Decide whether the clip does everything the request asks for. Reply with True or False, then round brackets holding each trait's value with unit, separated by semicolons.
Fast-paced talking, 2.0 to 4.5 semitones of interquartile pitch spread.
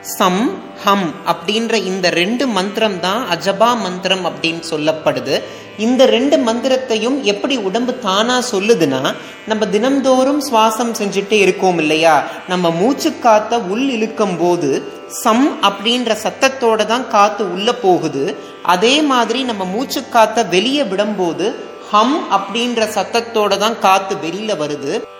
False (120 wpm; 4.2 semitones)